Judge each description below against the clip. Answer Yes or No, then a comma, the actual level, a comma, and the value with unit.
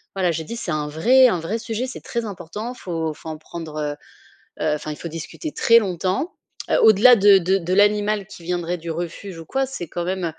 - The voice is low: No, medium, 185 Hz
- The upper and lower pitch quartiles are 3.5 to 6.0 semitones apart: Yes, average, 4.7 semitones